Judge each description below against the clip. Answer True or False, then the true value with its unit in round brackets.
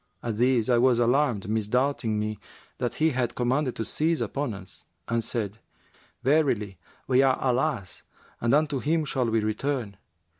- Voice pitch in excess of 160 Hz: False (125 Hz)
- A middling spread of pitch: True (3.9 semitones)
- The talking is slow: False (155 wpm)